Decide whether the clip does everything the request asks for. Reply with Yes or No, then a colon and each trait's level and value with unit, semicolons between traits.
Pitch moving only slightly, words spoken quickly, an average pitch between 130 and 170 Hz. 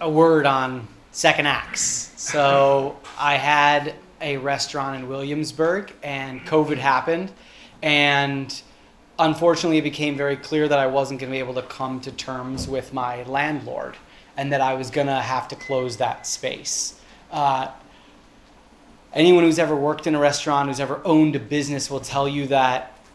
No: narrow, 2.1 semitones; average, 165 wpm; medium, 140 Hz